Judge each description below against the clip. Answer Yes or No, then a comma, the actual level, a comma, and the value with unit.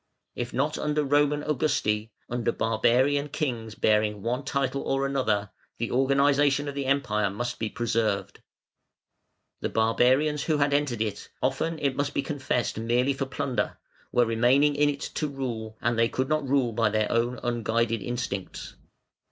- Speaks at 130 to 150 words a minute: No, average, 160 wpm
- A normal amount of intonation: Yes, average, 3.9 semitones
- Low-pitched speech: Yes, low, 125 Hz